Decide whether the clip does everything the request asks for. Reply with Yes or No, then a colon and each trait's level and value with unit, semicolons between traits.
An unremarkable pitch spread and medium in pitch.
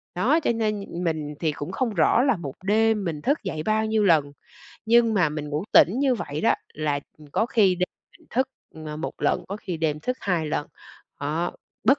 No: wide, 6.3 semitones; medium, 180 Hz